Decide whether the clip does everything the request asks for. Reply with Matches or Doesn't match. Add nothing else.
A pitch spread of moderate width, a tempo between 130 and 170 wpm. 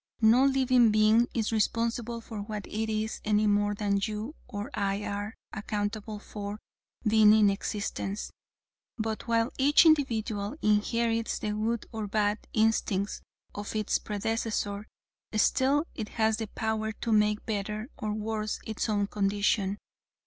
Doesn't match